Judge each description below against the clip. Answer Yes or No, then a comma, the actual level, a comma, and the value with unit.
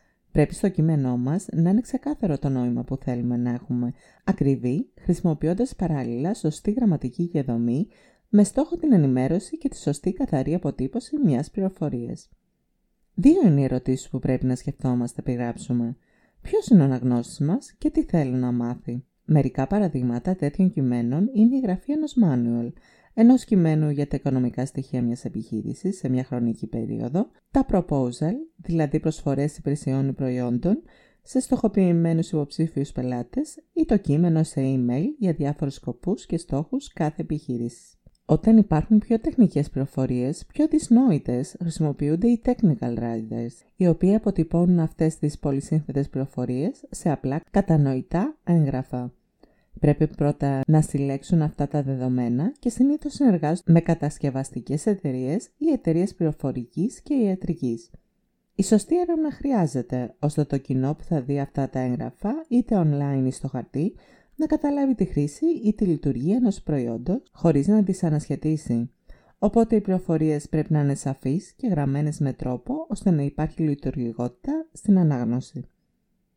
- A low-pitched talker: No, medium, 155 Hz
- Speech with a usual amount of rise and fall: No, wide, 7.3 semitones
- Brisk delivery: No, average, 140 wpm